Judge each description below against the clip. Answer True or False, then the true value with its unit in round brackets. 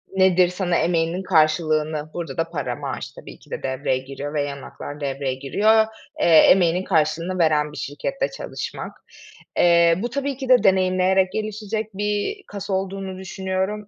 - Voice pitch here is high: False (180 Hz)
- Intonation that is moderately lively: True (4.1 semitones)